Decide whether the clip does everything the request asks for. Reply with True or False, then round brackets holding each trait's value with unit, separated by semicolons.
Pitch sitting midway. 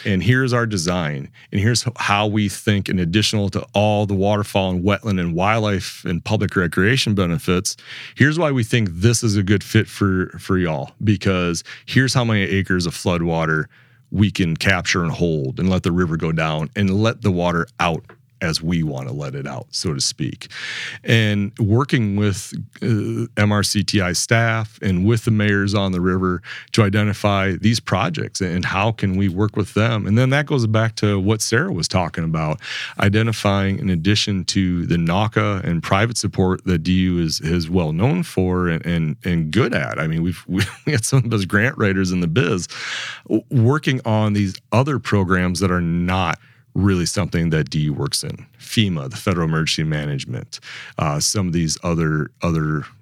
False (100 Hz)